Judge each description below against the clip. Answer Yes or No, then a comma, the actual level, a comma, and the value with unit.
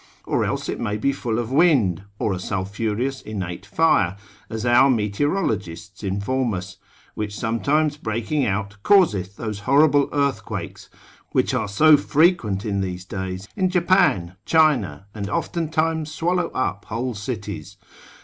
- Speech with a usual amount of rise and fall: No, wide, 6.7 semitones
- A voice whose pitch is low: Yes, low, 110 Hz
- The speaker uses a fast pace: No, average, 140 wpm